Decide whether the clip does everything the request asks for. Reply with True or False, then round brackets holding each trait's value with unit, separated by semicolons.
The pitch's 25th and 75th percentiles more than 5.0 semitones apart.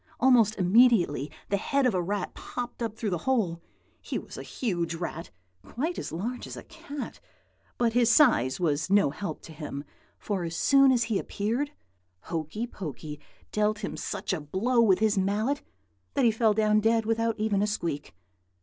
True (5.4 semitones)